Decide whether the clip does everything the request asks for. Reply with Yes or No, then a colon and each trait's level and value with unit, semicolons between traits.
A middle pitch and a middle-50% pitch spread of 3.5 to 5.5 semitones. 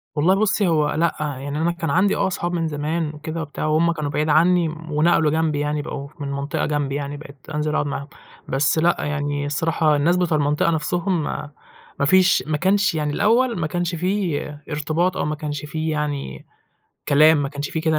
No: medium, 155 Hz; narrow, 2.5 semitones